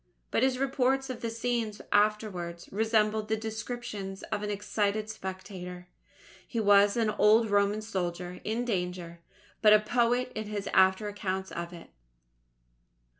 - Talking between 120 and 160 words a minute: Yes, average, 140 wpm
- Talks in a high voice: Yes, high, 210 Hz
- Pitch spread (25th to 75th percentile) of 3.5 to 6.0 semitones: No, average, 2.8 semitones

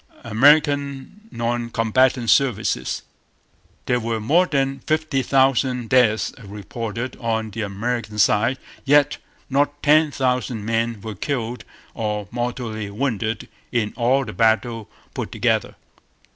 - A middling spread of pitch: Yes, average, 3.5 semitones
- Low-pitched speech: Yes, low, 120 Hz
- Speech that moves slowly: Yes, slow, 115 wpm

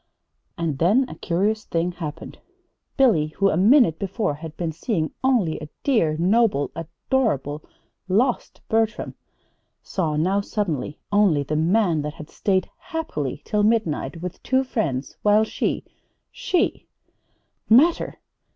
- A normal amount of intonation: No, wide, 6.2 semitones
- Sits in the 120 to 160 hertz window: No, medium, 185 Hz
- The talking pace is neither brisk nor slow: No, slow, 130 wpm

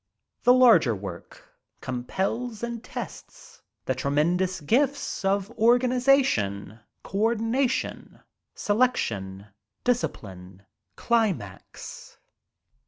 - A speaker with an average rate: No, slow, 75 wpm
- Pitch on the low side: No, high, 205 Hz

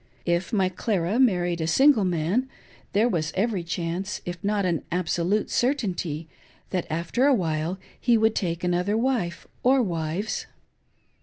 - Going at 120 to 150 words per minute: Yes, average, 145 wpm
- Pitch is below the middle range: No, medium, 185 Hz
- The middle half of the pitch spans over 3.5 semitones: Yes, average, 4.5 semitones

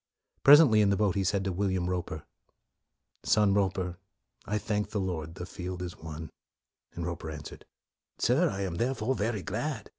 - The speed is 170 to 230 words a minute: Yes, average, 185 wpm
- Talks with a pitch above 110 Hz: No, very low, 95 Hz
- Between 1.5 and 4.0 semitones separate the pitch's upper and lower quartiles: Yes, average, 3.2 semitones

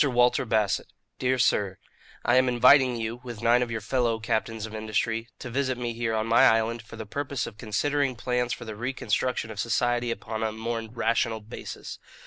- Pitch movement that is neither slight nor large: No, narrow, 1.9 semitones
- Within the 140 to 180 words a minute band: No, average, 190 wpm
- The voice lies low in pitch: Yes, low, 115 Hz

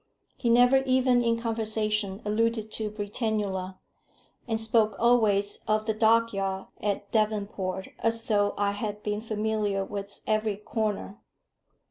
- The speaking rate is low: Yes, slow, 130 wpm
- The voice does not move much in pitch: Yes, narrow, 1.9 semitones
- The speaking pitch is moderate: No, high, 215 Hz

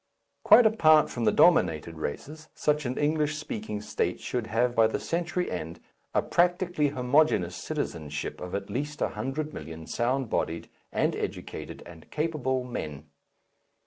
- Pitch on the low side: Yes, low, 125 Hz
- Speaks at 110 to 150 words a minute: Yes, average, 145 wpm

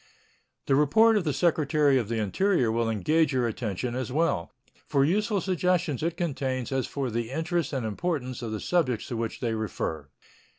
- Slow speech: No, average, 180 wpm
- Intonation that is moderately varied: No, wide, 6.1 semitones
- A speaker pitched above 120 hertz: Yes, low, 135 Hz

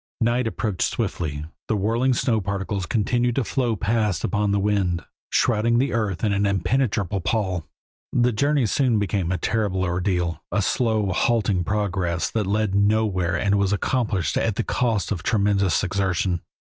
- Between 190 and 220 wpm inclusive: No, average, 155 wpm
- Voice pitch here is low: Yes, low, 100 Hz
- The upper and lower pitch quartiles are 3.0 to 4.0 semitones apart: Yes, average, 3.3 semitones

